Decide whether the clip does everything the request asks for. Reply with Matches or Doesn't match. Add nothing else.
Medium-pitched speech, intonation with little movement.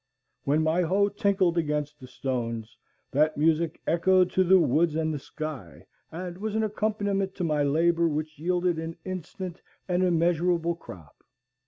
Doesn't match